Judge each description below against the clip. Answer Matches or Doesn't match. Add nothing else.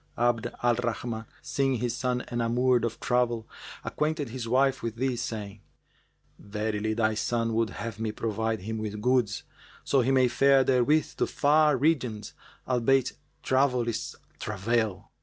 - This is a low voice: Matches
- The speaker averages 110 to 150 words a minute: Matches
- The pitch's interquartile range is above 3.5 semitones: Doesn't match